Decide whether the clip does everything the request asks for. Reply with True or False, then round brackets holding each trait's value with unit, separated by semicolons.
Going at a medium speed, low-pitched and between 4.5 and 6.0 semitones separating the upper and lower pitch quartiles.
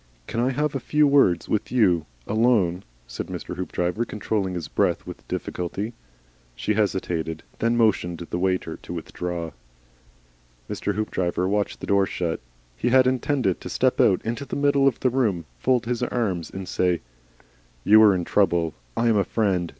True (175 wpm; 100 Hz; 5.2 semitones)